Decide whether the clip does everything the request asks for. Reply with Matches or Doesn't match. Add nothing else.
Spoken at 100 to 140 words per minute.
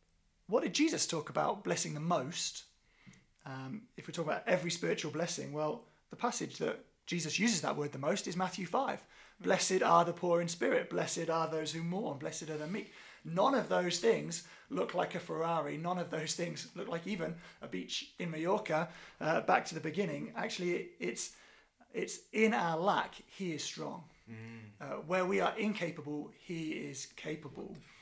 Doesn't match